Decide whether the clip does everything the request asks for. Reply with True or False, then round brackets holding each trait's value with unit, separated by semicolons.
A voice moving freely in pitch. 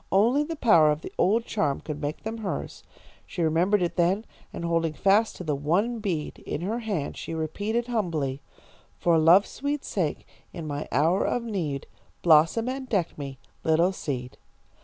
True (6.0 semitones)